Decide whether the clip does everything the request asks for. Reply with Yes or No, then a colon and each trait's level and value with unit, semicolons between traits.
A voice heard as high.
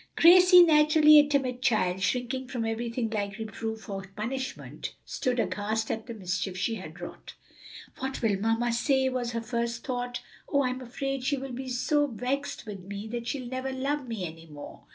Yes: high, 240 Hz